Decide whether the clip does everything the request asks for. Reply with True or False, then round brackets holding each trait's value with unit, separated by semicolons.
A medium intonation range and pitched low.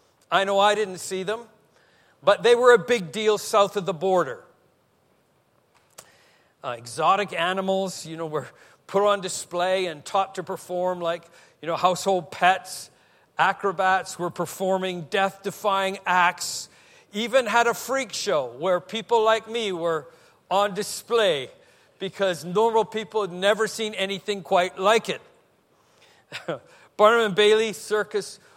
False (3.0 semitones; 195 Hz)